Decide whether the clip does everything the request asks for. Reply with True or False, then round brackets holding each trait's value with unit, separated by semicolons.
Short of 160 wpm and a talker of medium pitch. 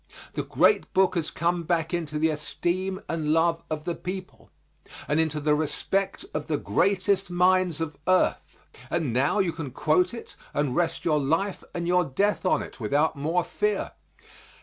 False (170 wpm; 170 Hz)